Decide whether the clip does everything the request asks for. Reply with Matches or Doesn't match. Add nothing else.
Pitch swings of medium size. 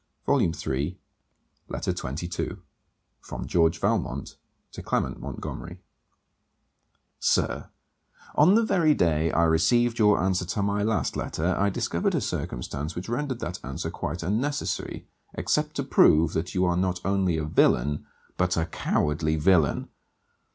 Matches